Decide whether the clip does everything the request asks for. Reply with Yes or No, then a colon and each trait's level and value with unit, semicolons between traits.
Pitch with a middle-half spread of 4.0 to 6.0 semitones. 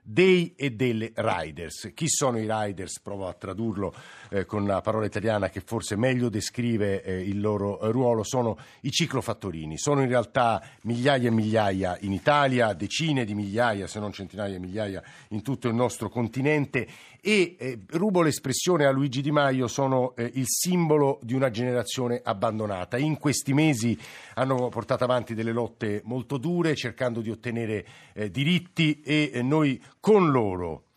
Yes: average, 4.6 semitones